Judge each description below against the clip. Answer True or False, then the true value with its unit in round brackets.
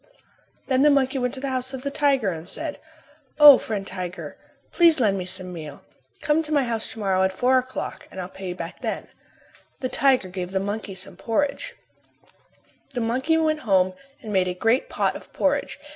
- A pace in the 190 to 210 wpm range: True (200 wpm)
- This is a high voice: True (235 Hz)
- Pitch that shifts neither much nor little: False (6.6 semitones)